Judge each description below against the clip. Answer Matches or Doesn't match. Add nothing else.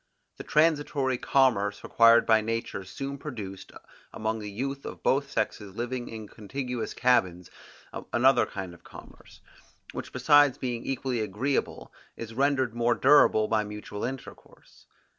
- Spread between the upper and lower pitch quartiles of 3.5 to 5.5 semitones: Matches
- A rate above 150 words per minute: Doesn't match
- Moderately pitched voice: Doesn't match